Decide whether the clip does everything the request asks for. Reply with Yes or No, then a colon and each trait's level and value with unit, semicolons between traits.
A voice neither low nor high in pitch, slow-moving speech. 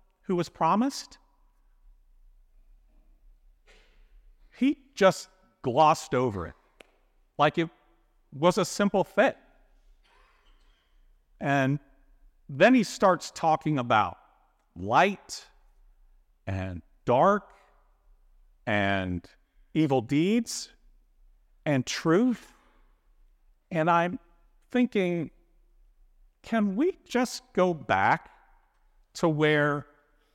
Yes: medium, 150 Hz; slow, 75 wpm